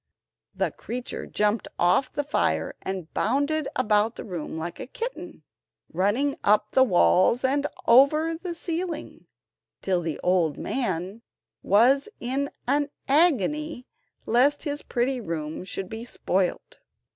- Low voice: No, high, 245 Hz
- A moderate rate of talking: No, slow, 130 wpm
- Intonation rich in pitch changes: Yes, wide, 7.1 semitones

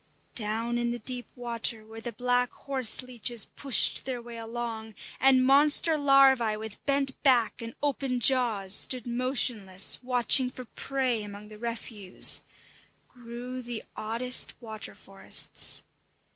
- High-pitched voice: Yes, high, 240 Hz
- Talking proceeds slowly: Yes, slow, 130 wpm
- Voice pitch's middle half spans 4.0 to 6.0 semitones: No, narrow, 2.4 semitones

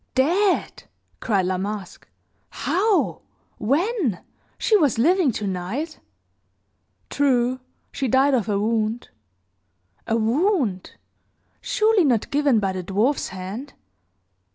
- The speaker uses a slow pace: Yes, slow, 105 wpm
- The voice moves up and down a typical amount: No, wide, 6.9 semitones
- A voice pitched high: Yes, very high, 250 Hz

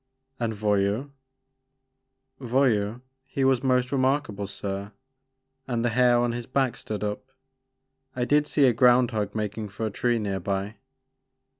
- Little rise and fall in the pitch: No, average, 3.6 semitones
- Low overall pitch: Yes, low, 120 Hz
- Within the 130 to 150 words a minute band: Yes, average, 145 wpm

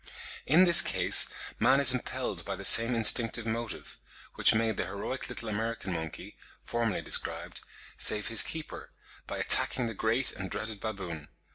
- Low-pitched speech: Yes, low, 115 Hz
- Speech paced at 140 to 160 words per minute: Yes, average, 155 wpm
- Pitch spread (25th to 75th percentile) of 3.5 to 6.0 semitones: No, average, 2.7 semitones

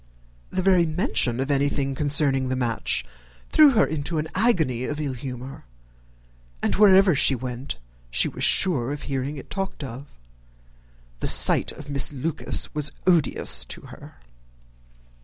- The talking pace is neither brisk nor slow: Yes, average, 145 wpm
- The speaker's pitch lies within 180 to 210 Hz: No, medium, 145 Hz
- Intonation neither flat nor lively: Yes, average, 4.2 semitones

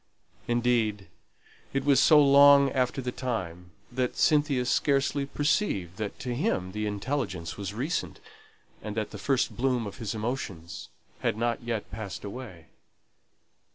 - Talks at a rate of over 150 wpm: No, average, 140 wpm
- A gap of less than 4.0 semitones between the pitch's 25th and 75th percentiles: No, average, 4.9 semitones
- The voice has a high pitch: No, low, 120 Hz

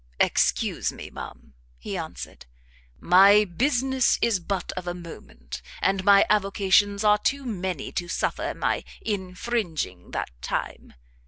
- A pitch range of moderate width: Yes, average, 3.2 semitones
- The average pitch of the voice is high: Yes, high, 195 Hz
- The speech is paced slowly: Yes, slow, 130 wpm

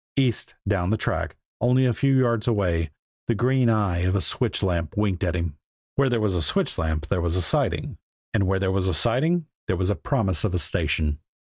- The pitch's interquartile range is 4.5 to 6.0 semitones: Yes, wide, 5.4 semitones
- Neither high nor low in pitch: No, low, 100 Hz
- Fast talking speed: Yes, fast, 215 wpm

